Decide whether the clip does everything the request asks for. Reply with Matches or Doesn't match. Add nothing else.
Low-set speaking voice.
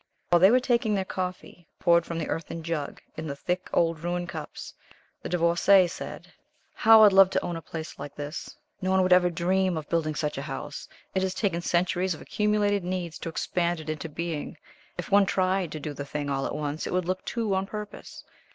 Doesn't match